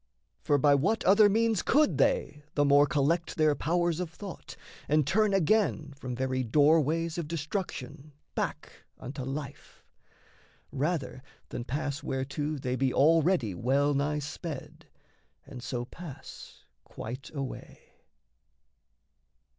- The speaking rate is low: Yes, slow, 125 wpm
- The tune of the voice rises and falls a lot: No, average, 3.8 semitones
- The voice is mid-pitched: Yes, medium, 150 Hz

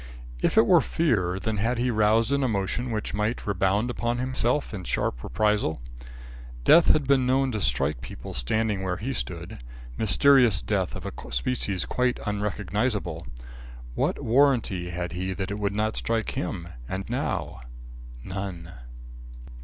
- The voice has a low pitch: Yes, low, 105 Hz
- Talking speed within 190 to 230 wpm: No, average, 150 wpm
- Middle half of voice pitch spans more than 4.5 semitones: Yes, average, 4.9 semitones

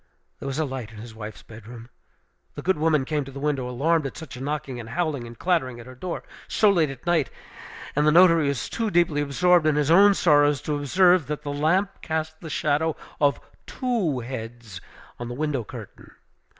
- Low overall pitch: No, medium, 145 Hz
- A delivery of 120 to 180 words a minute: No, fast, 205 wpm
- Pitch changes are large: No, average, 4.4 semitones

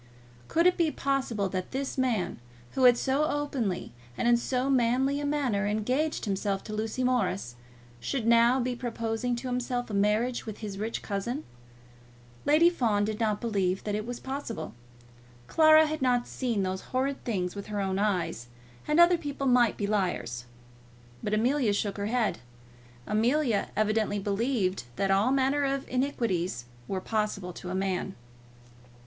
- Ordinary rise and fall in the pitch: Yes, average, 4.6 semitones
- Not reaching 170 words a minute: Yes, average, 160 wpm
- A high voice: Yes, high, 230 Hz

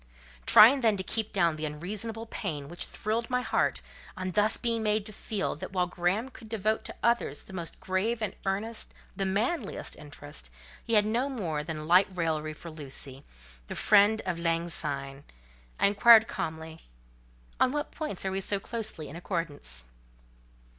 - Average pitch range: No, wide, 5.9 semitones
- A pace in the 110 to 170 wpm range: Yes, average, 165 wpm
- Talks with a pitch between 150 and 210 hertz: Yes, high, 190 Hz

